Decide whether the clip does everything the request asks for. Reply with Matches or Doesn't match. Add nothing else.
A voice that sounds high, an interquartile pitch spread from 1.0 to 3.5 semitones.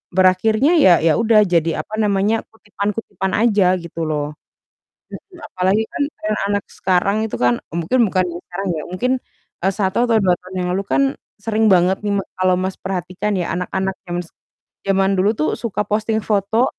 Matches